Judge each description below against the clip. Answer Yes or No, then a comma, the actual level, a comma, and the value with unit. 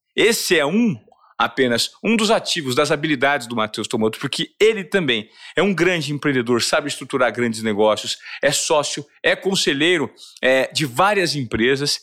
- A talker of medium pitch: Yes, medium, 145 Hz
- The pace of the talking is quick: No, average, 155 wpm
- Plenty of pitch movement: Yes, wide, 7.3 semitones